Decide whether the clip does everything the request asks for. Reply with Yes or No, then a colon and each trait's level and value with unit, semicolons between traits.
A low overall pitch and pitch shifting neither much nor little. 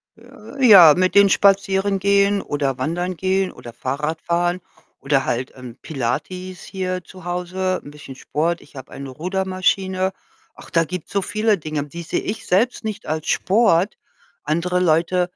No: medium, 180 Hz; average, 3.9 semitones